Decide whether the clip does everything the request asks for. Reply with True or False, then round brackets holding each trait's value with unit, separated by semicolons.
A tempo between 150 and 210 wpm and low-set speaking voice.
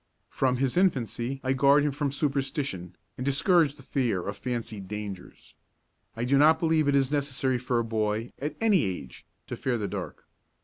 True (180 wpm; 130 Hz)